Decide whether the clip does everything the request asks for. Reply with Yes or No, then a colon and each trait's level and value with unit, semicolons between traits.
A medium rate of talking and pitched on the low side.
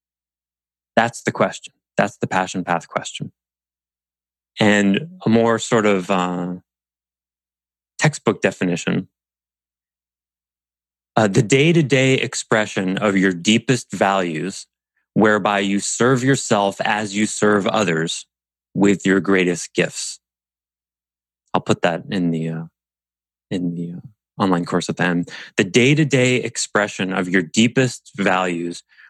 No: slow, 120 wpm; very low, 90 Hz